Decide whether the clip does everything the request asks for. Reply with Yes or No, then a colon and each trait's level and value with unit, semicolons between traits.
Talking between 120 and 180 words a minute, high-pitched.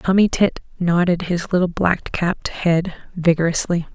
No: slow, 135 wpm; medium, 175 Hz